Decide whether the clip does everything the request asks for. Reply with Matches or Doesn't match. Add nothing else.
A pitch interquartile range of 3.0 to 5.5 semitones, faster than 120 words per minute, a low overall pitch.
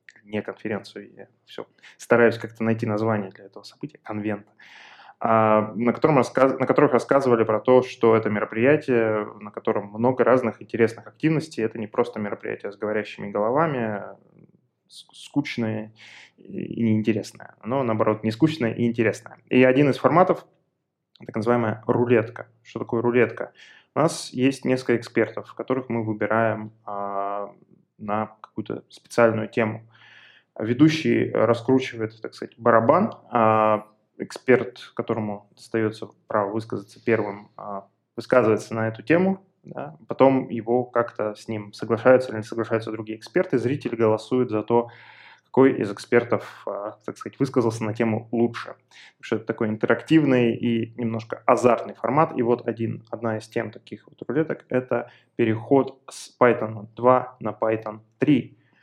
Doesn't match